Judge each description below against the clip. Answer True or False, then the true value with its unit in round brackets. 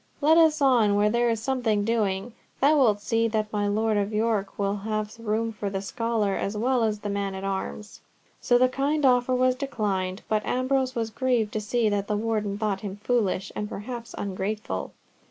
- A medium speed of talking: True (195 wpm)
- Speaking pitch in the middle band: False (215 Hz)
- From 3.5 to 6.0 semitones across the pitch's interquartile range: False (3.1 semitones)